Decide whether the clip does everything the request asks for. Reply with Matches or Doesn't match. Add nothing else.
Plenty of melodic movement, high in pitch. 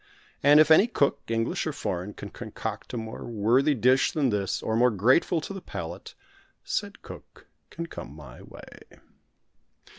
Doesn't match